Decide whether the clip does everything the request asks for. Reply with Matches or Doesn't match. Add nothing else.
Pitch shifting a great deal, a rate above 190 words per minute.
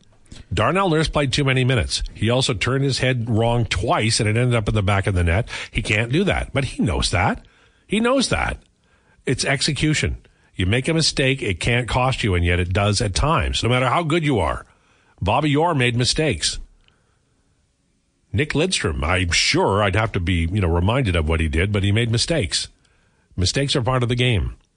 Matches